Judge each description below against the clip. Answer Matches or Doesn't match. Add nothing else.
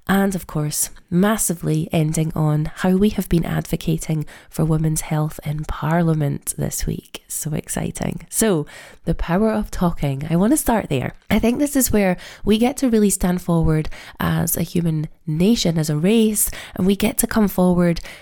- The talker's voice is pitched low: Doesn't match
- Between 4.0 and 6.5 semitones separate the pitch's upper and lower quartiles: Matches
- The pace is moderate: Matches